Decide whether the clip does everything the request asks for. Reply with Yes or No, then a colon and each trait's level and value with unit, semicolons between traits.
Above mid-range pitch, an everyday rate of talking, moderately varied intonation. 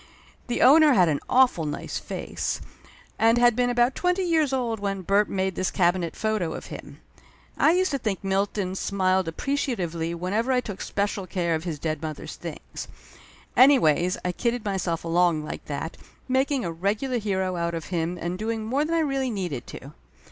No: high, 195 Hz; average, 180 wpm; wide, 6.3 semitones